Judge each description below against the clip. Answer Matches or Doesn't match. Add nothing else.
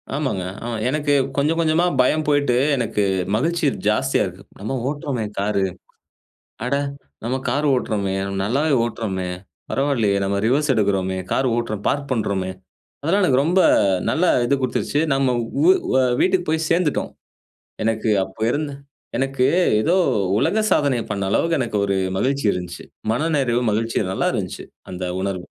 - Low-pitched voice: Matches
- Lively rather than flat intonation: Matches